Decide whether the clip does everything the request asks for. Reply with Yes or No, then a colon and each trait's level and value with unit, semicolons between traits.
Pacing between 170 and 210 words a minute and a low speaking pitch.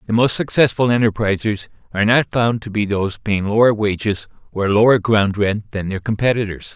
Yes: average, 180 wpm; low, 110 Hz